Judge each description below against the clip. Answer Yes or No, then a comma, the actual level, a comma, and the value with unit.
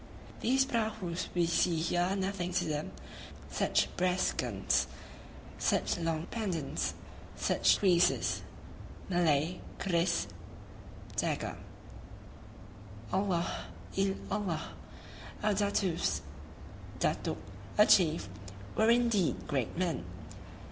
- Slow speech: Yes, slow, 95 wpm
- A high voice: No, medium, 180 Hz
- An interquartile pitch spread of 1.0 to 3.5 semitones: Yes, average, 3.1 semitones